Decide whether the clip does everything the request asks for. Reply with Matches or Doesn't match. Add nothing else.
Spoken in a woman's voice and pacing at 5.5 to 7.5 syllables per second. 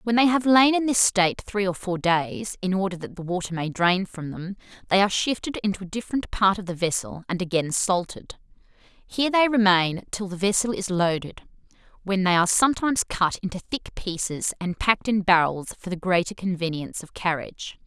Matches